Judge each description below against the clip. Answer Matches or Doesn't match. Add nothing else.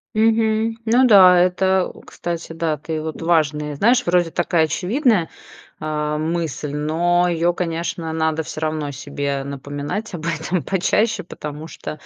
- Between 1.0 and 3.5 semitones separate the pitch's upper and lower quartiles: Matches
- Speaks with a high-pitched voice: Doesn't match